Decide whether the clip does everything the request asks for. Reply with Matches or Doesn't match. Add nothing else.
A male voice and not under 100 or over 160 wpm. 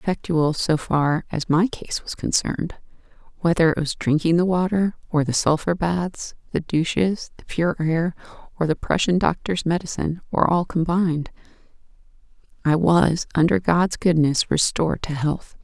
Doesn't match